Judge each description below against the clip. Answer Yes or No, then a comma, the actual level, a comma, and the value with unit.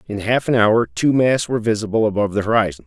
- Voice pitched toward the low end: Yes, low, 110 Hz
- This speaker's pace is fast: Yes, fast, 230 wpm